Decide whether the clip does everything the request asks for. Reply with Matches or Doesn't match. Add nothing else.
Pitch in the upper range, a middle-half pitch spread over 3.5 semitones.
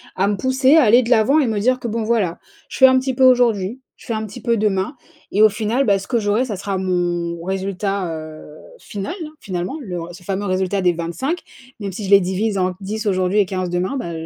Matches